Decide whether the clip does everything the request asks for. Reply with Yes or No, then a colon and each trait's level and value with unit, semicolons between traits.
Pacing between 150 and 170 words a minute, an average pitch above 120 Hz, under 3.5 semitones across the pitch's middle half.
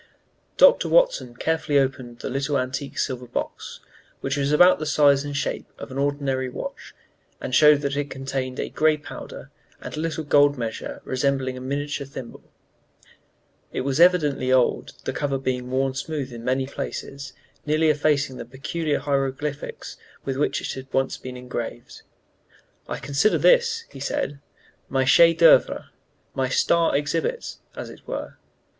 Yes: average, 160 wpm; medium, 140 Hz; narrow, 2.4 semitones